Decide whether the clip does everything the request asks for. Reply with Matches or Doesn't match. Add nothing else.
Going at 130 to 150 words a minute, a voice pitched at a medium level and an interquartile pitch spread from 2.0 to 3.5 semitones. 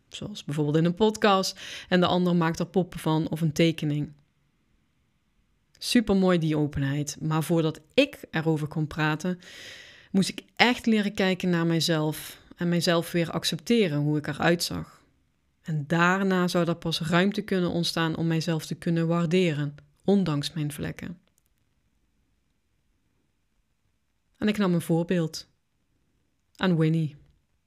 Matches